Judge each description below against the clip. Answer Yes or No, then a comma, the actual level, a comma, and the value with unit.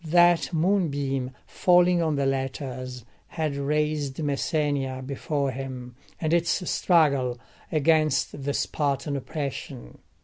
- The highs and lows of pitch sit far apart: No, average, 3.0 semitones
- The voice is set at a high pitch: No, medium, 145 Hz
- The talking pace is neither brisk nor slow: No, slow, 105 wpm